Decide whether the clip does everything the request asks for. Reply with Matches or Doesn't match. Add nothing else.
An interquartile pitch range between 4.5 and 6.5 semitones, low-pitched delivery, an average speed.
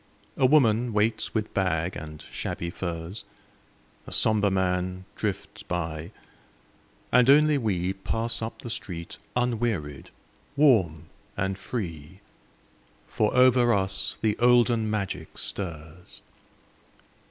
Doesn't match